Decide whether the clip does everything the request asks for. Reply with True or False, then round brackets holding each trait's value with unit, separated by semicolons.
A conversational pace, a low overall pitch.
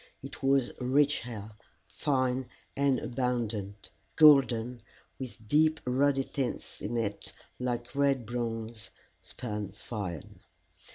False (105 wpm; 125 Hz)